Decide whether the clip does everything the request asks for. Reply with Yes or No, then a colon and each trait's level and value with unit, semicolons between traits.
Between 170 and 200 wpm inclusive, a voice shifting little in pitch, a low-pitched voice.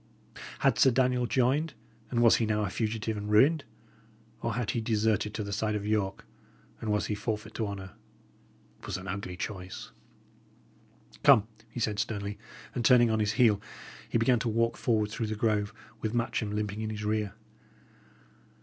Yes: average, 175 wpm; narrow, 1.9 semitones; low, 110 Hz